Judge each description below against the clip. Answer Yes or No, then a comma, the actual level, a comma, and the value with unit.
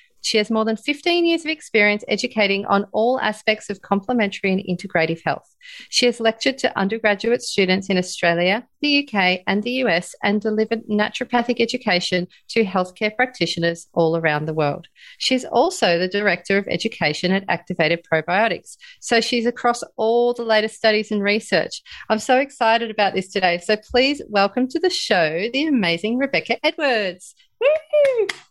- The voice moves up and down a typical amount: Yes, average, 4.9 semitones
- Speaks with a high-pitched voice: Yes, high, 215 Hz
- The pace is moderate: Yes, average, 160 wpm